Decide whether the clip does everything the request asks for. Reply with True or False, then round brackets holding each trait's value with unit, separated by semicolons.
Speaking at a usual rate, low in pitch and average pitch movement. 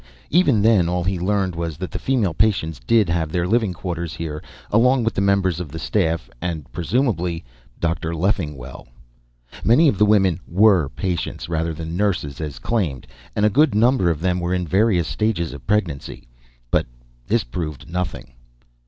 True (170 wpm; 90 Hz; 4.3 semitones)